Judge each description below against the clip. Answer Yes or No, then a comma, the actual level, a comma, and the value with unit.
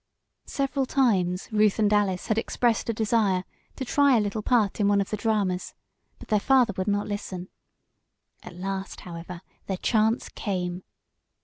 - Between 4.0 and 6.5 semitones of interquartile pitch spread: No, average, 3.2 semitones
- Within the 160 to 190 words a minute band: Yes, average, 165 wpm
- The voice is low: No, high, 205 Hz